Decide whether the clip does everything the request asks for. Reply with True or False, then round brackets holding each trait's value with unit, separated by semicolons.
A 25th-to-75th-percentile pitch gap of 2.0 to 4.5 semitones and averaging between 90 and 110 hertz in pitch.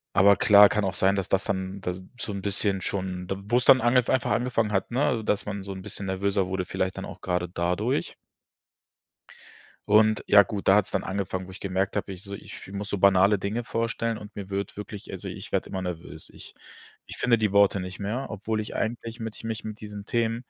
True (2.4 semitones; 100 Hz)